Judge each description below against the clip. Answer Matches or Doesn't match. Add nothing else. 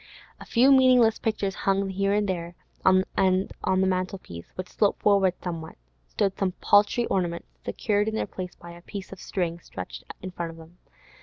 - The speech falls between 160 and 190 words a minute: Matches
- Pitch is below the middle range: Doesn't match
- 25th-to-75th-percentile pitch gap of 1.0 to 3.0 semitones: Matches